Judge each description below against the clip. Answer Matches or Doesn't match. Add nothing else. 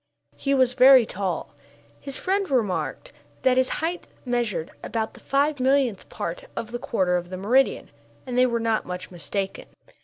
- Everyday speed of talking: Matches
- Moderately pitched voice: Doesn't match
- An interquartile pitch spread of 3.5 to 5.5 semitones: Matches